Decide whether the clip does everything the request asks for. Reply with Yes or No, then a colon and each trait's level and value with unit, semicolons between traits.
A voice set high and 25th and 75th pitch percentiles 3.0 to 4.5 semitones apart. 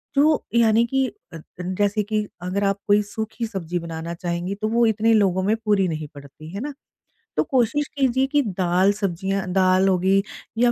Yes: high, 200 Hz; average, 3.9 semitones